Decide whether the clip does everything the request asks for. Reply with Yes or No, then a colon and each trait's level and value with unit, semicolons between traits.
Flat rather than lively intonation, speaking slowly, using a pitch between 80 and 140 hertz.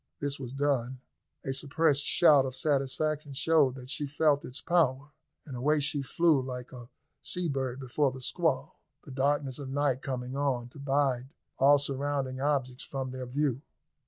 No: narrow, 1.9 semitones; average, 165 wpm; low, 135 Hz